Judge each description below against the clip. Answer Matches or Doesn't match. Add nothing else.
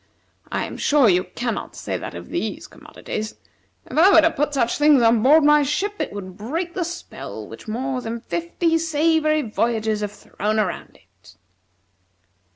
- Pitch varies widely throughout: Matches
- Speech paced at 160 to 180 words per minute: Matches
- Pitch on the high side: Matches